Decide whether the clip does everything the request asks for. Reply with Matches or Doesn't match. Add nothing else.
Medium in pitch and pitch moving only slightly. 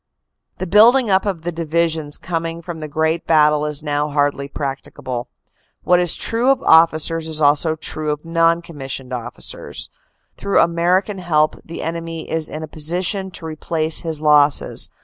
Matches